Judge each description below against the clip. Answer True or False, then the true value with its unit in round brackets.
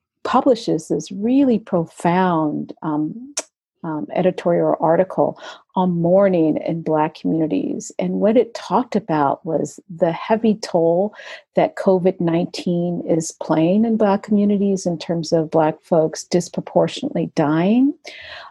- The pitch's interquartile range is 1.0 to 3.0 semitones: False (4.5 semitones)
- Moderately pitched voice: True (180 Hz)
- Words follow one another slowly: True (120 wpm)